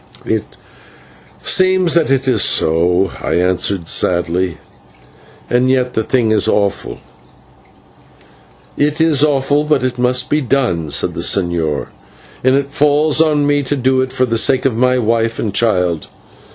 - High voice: No, low, 125 Hz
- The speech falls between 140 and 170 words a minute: Yes, average, 150 wpm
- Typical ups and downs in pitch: No, wide, 6.5 semitones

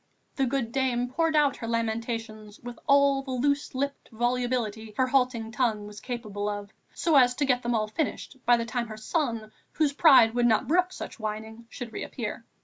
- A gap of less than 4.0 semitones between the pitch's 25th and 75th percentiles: Yes, average, 3.5 semitones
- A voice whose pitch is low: No, high, 240 Hz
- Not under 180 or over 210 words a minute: Yes, average, 190 wpm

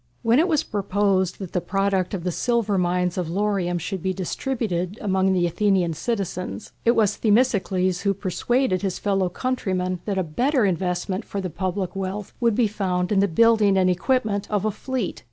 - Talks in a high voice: Yes, high, 195 Hz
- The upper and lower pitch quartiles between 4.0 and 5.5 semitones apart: No, average, 2.7 semitones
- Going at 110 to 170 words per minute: No, average, 185 wpm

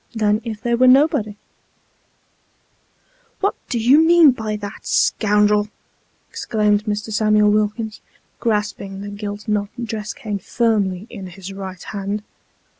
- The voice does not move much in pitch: Yes, narrow, 2.0 semitones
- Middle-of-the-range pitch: No, high, 210 Hz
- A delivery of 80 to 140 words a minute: Yes, slow, 135 wpm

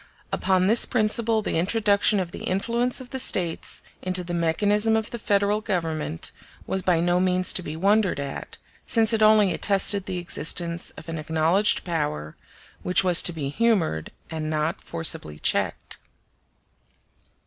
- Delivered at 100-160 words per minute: Yes, average, 155 wpm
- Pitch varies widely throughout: No, average, 4.4 semitones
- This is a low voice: No, medium, 185 Hz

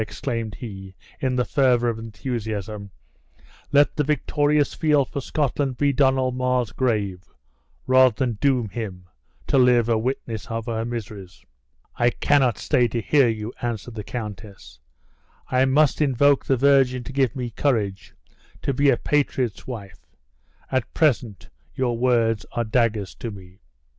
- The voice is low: Yes, low, 120 Hz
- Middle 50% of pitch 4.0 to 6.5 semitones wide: No, average, 3.4 semitones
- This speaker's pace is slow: No, average, 150 wpm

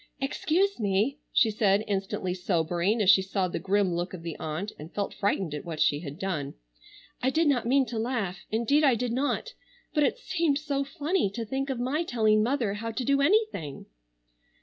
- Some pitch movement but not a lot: No, wide, 6.6 semitones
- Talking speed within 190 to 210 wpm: Yes, average, 195 wpm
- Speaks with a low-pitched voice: No, high, 220 Hz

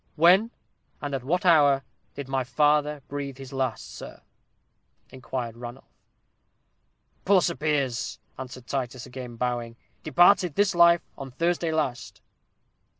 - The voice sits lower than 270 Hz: Yes, medium, 140 Hz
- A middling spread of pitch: Yes, average, 4.4 semitones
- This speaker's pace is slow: Yes, slow, 125 wpm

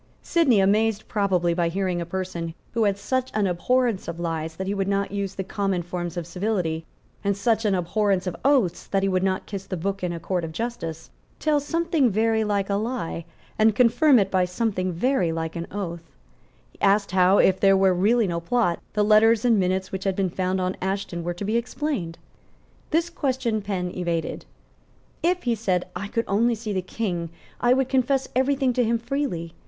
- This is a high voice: Yes, high, 195 Hz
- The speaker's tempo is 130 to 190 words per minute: No, average, 200 wpm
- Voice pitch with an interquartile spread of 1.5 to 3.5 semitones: No, average, 4.2 semitones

